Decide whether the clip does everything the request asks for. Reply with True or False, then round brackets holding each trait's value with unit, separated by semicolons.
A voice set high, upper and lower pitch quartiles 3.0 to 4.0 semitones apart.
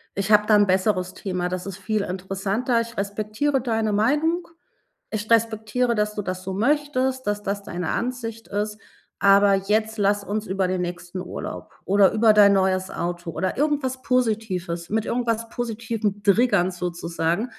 True (210 Hz; 3.3 semitones)